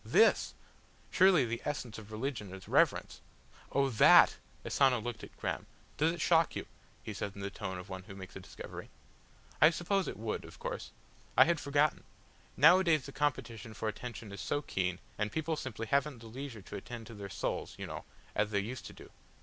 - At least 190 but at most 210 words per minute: Yes, average, 200 wpm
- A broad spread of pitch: Yes, wide, 5.9 semitones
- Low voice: Yes, low, 120 Hz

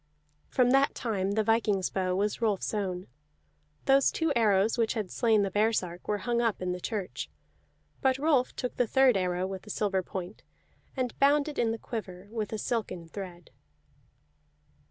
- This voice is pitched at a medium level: No, high, 215 Hz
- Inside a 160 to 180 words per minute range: Yes, average, 175 wpm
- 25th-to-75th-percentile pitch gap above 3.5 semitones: Yes, average, 4.1 semitones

